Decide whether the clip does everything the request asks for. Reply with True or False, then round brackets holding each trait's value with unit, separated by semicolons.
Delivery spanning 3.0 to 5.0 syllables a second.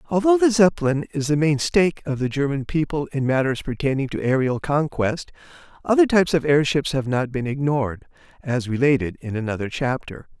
False (5.6 syllables/s)